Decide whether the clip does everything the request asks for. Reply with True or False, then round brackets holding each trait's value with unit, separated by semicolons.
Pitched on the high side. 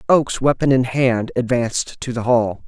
False (125 Hz)